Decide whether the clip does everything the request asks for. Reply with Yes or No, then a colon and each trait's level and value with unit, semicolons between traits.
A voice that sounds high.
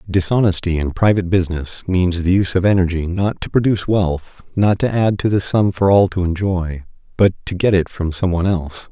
No: very low, 95 Hz